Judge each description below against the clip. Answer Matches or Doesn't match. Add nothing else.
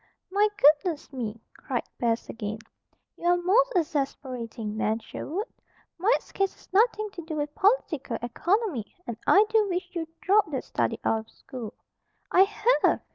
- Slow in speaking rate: Doesn't match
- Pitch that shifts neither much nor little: Doesn't match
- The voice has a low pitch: Doesn't match